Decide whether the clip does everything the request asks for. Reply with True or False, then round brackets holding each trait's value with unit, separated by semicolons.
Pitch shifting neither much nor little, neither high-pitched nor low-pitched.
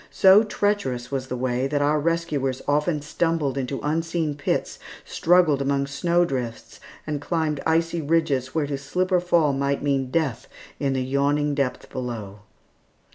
True (3.5 semitones; 145 Hz)